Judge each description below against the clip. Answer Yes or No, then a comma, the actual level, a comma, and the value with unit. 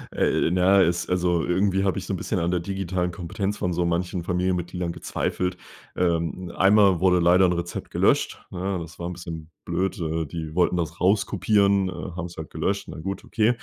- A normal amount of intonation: No, narrow, 1.9 semitones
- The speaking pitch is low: Yes, very low, 90 Hz